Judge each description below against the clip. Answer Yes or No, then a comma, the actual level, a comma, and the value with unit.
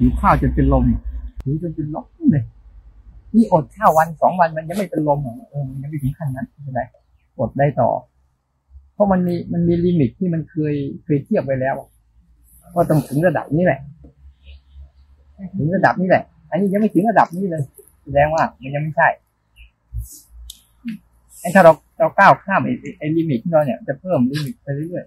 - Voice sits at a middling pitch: Yes, medium, 145 Hz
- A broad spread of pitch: Yes, wide, 6.9 semitones